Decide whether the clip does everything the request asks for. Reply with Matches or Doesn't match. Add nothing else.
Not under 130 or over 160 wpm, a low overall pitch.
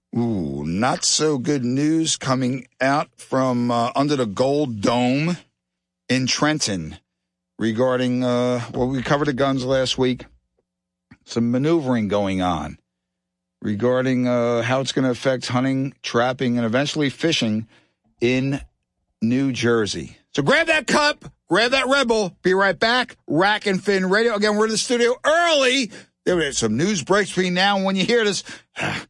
Matches